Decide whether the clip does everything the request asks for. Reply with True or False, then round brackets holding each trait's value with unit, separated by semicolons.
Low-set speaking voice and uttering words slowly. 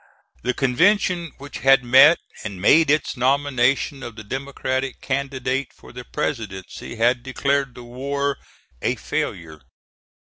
True (130 Hz; 130 wpm)